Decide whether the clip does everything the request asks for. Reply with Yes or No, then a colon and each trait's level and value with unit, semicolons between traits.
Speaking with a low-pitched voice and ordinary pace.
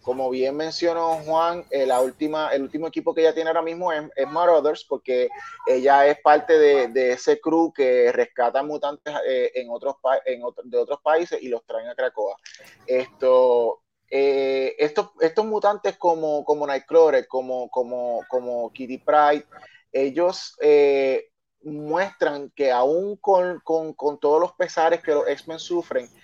No: medium, 160 Hz; average, 160 wpm